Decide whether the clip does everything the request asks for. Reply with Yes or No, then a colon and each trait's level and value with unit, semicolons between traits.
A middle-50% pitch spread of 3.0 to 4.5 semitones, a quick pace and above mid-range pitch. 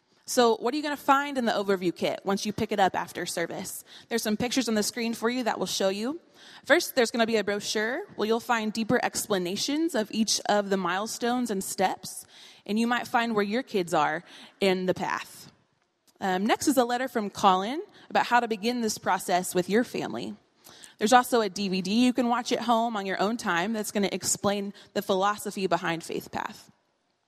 Yes: average, 3.6 semitones; fast, 215 wpm; high, 220 Hz